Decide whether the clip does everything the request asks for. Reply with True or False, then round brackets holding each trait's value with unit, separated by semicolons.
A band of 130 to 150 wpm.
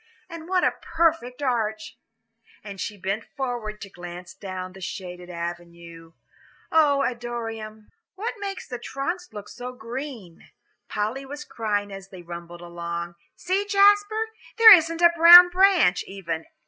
True (140 wpm)